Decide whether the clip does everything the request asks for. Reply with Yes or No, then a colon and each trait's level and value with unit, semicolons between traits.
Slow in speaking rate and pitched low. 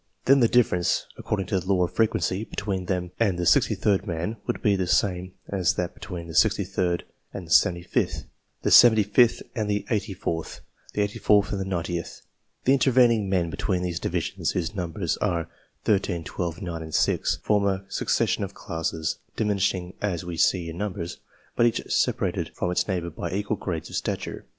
No: average, 180 wpm; very low, 95 Hz